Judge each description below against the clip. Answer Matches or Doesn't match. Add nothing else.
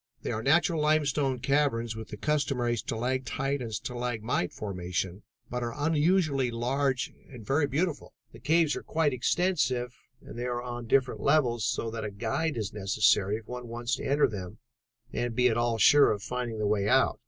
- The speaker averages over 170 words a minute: Matches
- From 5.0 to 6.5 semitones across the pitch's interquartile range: Doesn't match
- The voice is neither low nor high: Doesn't match